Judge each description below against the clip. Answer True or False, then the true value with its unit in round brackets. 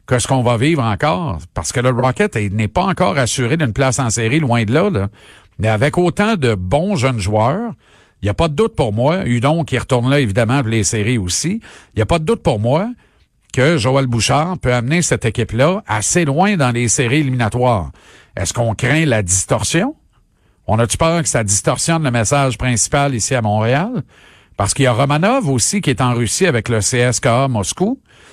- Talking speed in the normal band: True (210 wpm)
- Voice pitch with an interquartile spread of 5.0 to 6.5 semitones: True (5.3 semitones)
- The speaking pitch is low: True (130 Hz)